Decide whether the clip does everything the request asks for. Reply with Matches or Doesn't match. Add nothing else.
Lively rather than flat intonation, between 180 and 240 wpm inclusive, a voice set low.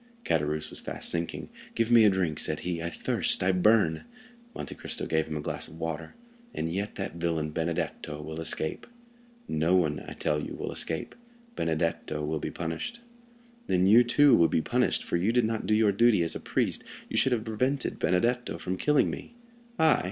Matches